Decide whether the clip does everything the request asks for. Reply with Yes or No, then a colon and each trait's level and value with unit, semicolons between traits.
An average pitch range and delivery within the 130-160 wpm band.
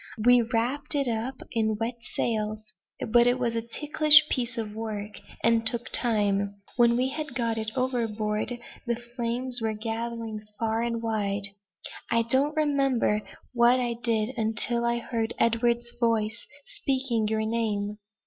No: narrow, 1.9 semitones; average, 150 wpm